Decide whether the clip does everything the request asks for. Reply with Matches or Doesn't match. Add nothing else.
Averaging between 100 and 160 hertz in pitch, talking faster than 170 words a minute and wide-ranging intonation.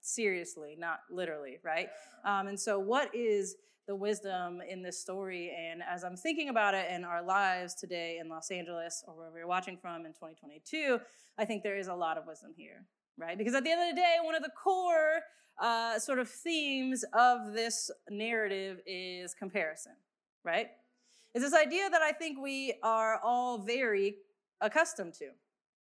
Doesn't match